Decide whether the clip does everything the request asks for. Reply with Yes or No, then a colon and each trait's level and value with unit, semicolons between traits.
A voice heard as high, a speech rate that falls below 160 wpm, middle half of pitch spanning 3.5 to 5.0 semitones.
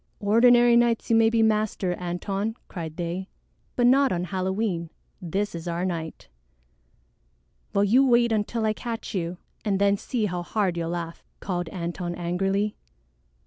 Yes: high, 195 Hz; average, 150 wpm; average, 4.2 semitones